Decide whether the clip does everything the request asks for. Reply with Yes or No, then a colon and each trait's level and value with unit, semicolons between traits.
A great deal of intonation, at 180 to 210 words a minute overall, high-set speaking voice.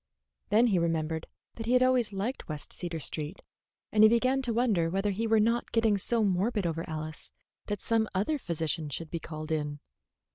Yes: wide, 5.8 semitones; average, 190 wpm; high, 195 Hz